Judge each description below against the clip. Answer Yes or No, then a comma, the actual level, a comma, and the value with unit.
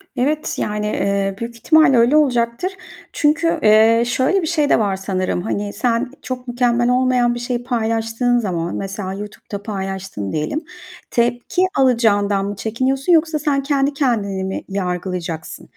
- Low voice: No, high, 235 Hz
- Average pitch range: Yes, average, 4.6 semitones